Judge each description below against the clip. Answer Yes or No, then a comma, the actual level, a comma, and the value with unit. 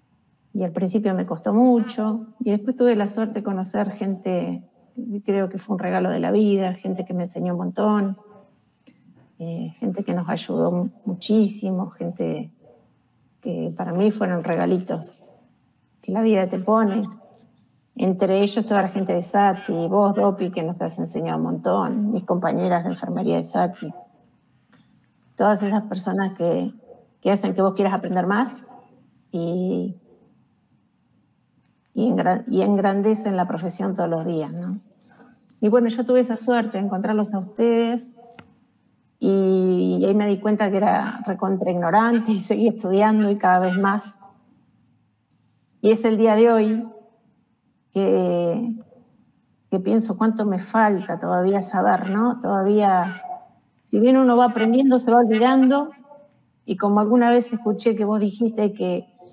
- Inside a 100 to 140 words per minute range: No, average, 150 wpm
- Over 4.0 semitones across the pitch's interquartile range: No, average, 3.4 semitones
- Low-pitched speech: No, high, 205 Hz